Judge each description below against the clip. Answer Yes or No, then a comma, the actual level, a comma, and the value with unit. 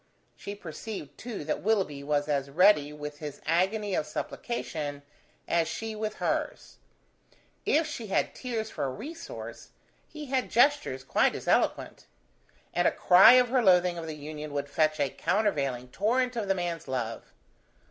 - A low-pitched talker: No, medium, 175 Hz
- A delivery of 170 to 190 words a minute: No, average, 160 wpm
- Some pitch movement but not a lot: No, wide, 7.0 semitones